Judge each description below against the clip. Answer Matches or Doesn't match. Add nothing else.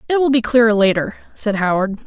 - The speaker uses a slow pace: Doesn't match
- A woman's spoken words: Matches